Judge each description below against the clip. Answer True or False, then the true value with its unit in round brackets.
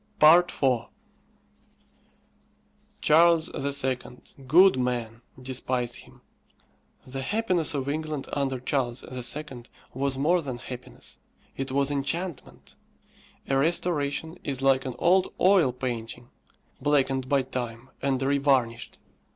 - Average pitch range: True (3.1 semitones)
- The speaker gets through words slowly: True (105 wpm)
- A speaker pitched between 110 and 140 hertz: True (135 Hz)